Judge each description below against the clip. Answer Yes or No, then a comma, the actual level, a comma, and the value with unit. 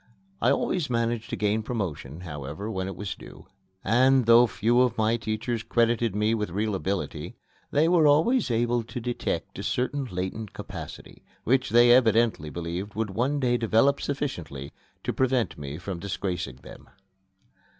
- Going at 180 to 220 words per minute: No, average, 160 wpm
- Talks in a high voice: No, low, 115 Hz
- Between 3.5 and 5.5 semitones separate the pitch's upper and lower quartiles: Yes, average, 4.1 semitones